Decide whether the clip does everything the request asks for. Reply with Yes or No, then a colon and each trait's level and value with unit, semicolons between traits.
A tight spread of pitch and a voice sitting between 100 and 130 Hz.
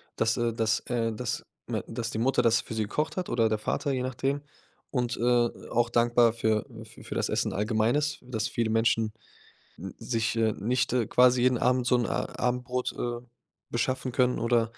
Yes: narrow, 1.8 semitones; low, 120 Hz